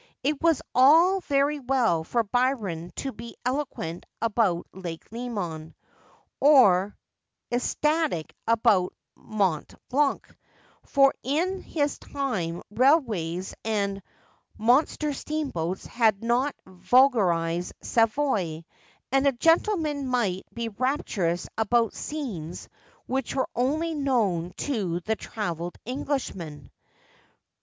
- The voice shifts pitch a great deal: Yes, wide, 7.3 semitones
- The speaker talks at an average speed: No, slow, 100 wpm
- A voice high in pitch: Yes, high, 235 Hz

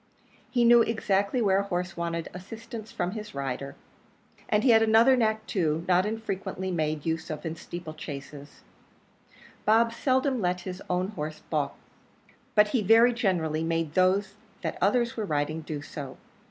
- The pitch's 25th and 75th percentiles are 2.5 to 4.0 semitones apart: No, wide, 5.4 semitones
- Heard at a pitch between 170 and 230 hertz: Yes, high, 190 Hz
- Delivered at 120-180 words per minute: Yes, average, 160 wpm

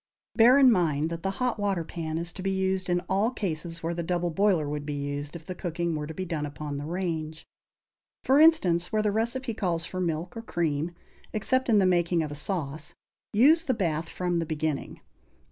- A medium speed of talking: No, fast, 215 wpm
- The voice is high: No, medium, 175 Hz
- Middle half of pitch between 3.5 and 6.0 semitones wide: Yes, average, 4.1 semitones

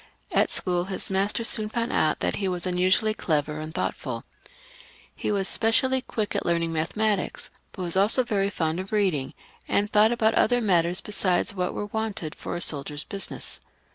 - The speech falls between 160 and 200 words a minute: Yes, average, 175 wpm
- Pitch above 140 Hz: Yes, high, 190 Hz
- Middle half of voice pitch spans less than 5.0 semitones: Yes, average, 4.0 semitones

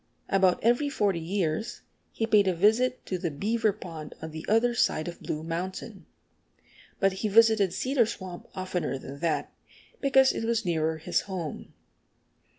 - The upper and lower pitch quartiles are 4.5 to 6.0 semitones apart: Yes, average, 5.2 semitones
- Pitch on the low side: No, high, 190 Hz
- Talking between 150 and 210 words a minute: Yes, average, 155 wpm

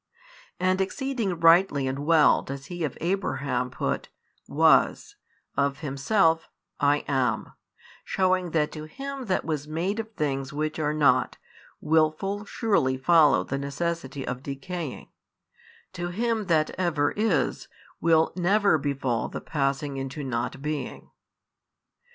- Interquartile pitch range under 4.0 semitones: No, average, 4.8 semitones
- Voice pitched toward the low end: No, medium, 155 Hz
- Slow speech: Yes, slow, 130 wpm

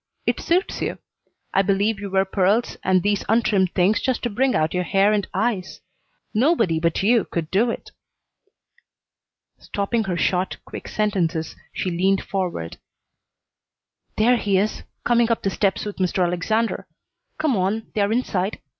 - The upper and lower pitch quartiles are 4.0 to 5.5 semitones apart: No, average, 3.3 semitones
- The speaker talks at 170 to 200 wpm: No, average, 155 wpm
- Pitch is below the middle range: No, high, 200 Hz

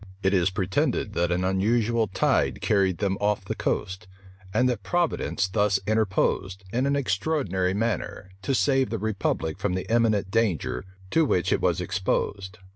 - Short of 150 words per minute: No, average, 160 wpm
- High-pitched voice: No, low, 100 Hz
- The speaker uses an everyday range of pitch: Yes, average, 3.5 semitones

